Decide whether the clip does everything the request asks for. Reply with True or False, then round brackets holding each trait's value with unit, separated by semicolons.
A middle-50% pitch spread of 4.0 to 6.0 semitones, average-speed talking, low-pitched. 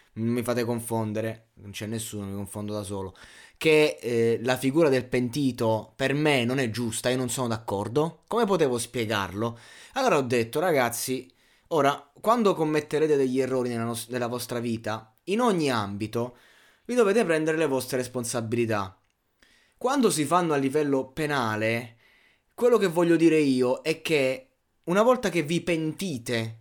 True (5.1 semitones; 160 wpm; 125 Hz)